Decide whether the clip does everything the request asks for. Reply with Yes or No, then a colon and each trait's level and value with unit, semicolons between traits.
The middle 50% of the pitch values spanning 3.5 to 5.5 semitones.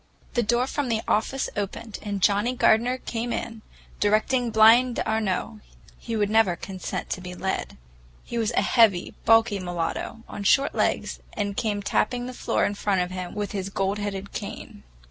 No: average, 2.7 semitones